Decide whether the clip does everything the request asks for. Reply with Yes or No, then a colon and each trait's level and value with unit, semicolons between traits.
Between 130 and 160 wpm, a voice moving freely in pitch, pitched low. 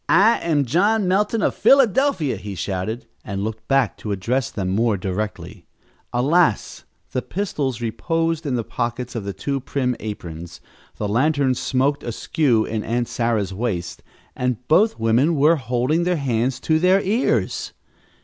Yes: average, 150 wpm; wide, 6.3 semitones; low, 125 Hz